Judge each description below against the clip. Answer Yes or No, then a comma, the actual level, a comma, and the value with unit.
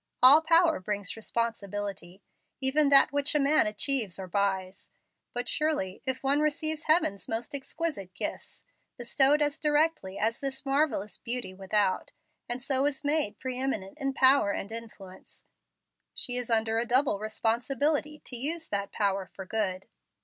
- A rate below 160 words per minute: Yes, average, 150 wpm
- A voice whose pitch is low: No, high, 245 Hz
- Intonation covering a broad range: Yes, wide, 6.1 semitones